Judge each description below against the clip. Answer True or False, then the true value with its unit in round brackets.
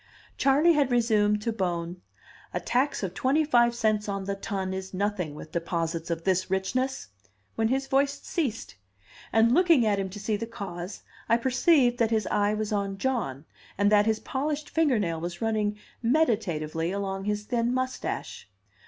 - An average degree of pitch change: True (4.7 semitones)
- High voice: True (215 Hz)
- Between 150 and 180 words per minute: True (170 wpm)